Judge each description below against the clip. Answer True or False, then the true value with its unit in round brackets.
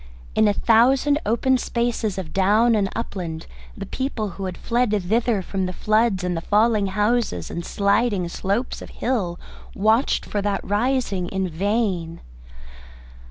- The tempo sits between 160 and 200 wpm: False (150 wpm)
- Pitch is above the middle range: True (205 Hz)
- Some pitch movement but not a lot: True (3.8 semitones)